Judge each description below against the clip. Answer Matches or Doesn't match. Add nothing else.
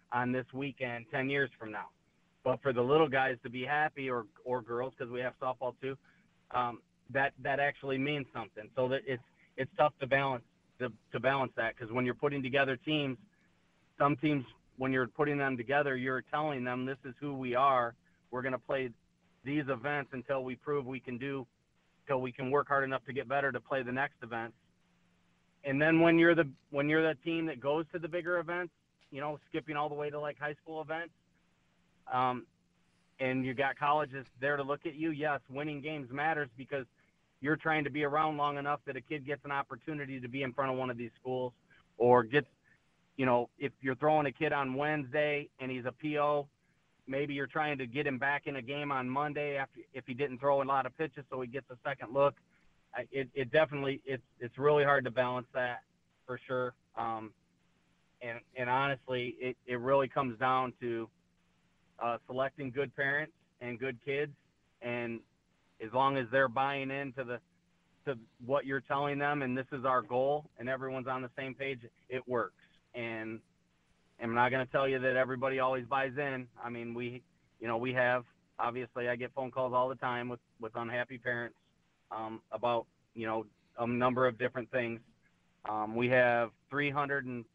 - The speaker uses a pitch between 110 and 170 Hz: Matches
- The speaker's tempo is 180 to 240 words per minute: Matches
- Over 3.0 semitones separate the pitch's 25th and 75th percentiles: Doesn't match